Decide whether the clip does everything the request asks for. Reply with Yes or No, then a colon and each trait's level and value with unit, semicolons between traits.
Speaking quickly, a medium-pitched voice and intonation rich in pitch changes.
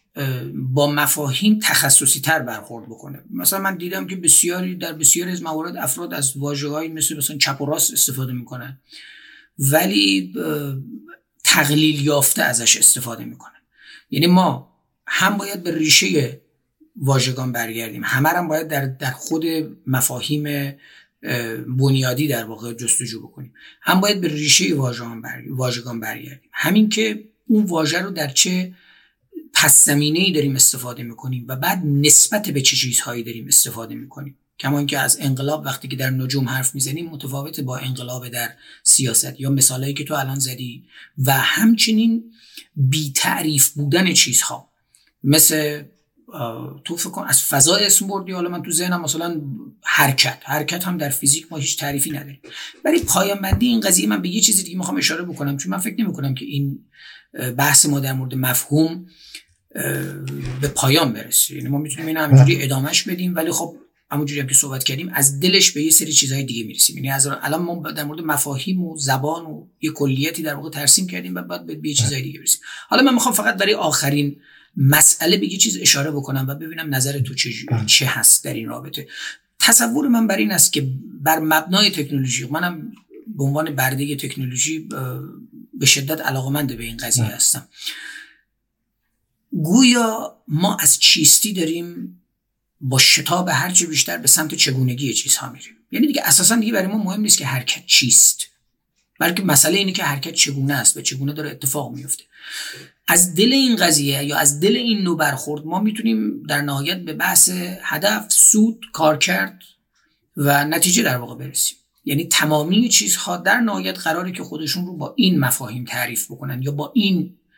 No: fast, 165 wpm; medium, 150 Hz; average, 4.3 semitones